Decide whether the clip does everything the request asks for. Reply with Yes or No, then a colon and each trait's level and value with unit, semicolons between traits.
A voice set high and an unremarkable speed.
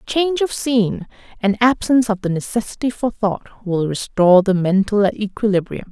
Yes: high, 210 Hz; average, 150 wpm